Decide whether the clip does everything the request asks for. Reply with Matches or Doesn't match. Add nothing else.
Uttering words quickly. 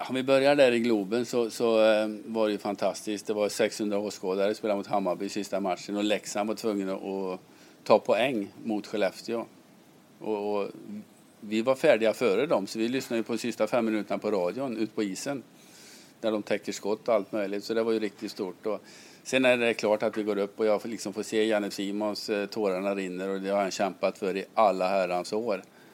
Matches